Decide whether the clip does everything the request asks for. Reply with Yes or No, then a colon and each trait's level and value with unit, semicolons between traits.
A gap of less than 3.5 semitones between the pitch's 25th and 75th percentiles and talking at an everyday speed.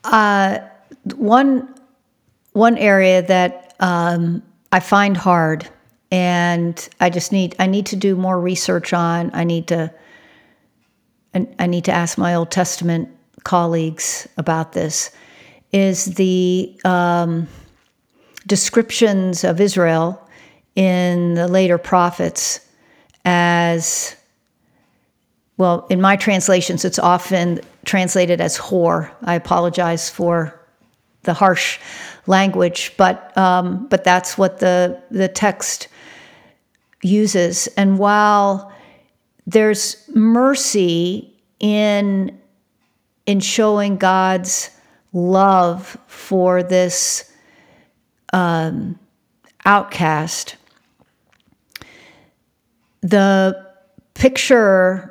No: narrow, 2.5 semitones; slow, 90 wpm